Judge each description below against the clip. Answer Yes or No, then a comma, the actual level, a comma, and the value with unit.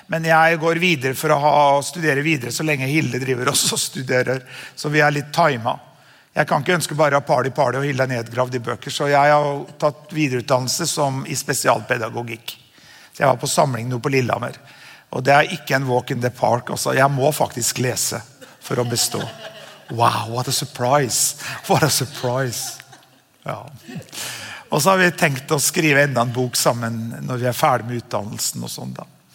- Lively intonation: No, average, 3.3 semitones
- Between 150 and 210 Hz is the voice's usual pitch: No, low, 135 Hz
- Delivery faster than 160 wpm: Yes, fast, 205 wpm